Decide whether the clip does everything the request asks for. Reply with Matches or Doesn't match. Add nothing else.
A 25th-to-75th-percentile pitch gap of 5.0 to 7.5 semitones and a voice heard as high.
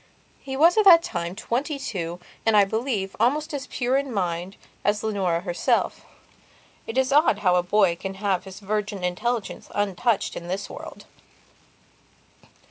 Matches